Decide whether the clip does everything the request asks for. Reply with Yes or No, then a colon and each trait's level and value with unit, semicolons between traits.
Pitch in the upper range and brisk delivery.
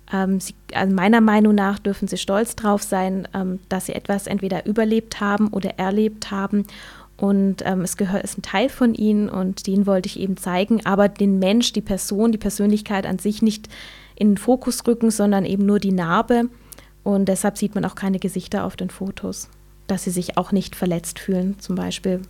Yes: high, 200 Hz; fast, 195 wpm